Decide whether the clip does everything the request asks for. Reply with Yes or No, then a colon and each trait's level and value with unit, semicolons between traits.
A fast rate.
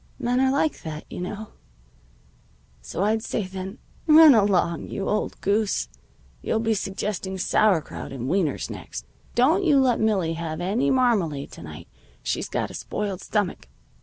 No: average, 155 wpm